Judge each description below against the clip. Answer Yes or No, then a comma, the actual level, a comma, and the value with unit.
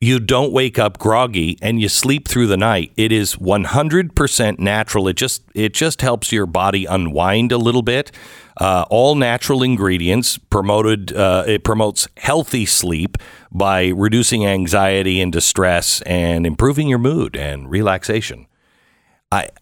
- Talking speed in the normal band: Yes, average, 145 wpm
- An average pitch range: Yes, average, 4.7 semitones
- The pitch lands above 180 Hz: No, low, 105 Hz